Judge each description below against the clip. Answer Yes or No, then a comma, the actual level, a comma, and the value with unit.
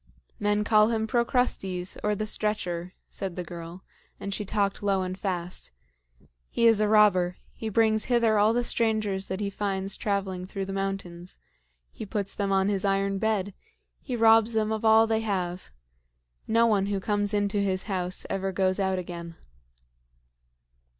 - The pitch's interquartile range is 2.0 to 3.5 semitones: Yes, narrow, 2.4 semitones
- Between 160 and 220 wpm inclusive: Yes, average, 165 wpm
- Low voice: No, high, 200 Hz